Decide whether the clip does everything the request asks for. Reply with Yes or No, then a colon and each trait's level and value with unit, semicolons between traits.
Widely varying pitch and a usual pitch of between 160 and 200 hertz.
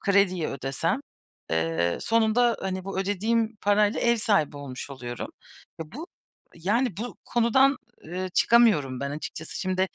Yes: wide, 7.4 semitones; high, 190 Hz